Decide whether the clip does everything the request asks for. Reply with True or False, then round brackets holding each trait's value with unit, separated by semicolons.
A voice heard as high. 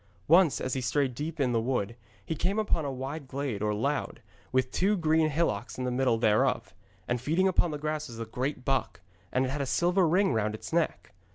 False (135 Hz)